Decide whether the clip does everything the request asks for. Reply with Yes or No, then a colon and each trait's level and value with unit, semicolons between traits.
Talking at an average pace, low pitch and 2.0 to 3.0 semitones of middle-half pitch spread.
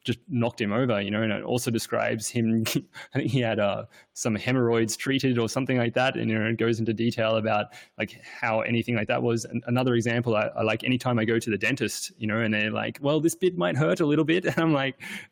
No: fast, 255 wpm; low, 115 Hz; average, 2.7 semitones